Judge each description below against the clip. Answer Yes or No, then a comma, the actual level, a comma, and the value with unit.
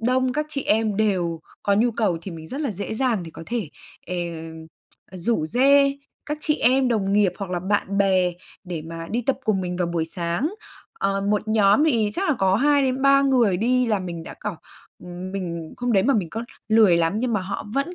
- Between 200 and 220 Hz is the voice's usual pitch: Yes, high, 210 Hz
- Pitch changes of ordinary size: No, wide, 5.8 semitones